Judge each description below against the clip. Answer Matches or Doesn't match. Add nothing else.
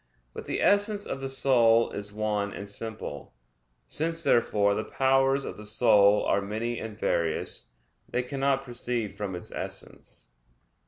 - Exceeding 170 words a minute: Doesn't match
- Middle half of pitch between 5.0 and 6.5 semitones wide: Doesn't match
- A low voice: Matches